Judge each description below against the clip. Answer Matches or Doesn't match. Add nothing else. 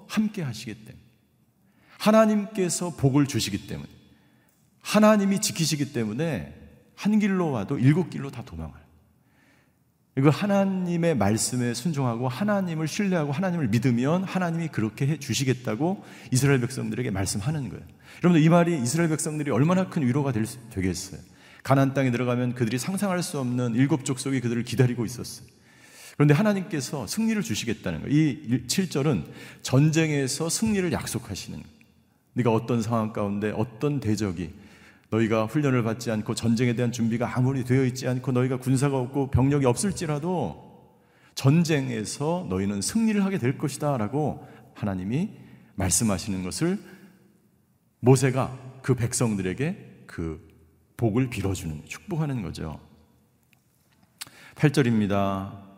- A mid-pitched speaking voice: Doesn't match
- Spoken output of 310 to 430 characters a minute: Matches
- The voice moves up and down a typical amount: Doesn't match